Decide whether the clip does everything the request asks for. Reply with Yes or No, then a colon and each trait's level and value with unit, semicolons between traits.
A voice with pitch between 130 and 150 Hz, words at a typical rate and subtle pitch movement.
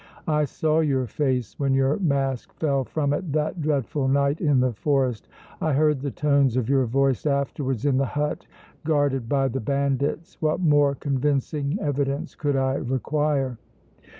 Yes: medium, 140 Hz; average, 160 wpm; narrow, 1.9 semitones